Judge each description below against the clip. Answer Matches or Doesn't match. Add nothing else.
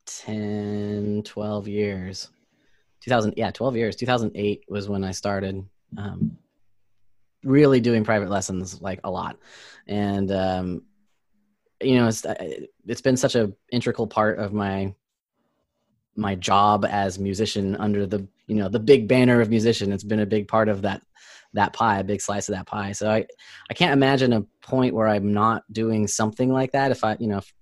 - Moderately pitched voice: Doesn't match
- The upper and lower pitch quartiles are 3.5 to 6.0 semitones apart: Doesn't match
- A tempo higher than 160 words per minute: Matches